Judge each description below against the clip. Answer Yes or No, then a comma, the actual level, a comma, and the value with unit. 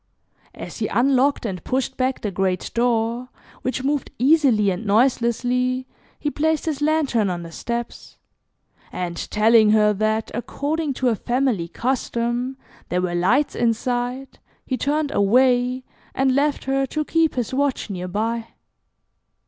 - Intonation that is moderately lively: Yes, average, 3.8 semitones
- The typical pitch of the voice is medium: No, high, 245 Hz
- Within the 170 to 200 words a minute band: No, average, 140 wpm